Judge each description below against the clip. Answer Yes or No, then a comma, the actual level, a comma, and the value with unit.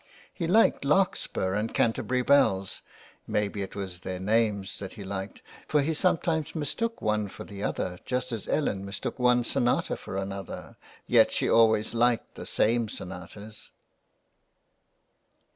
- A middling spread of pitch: Yes, average, 4.5 semitones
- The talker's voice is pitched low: Yes, low, 110 Hz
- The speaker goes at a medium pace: Yes, average, 145 wpm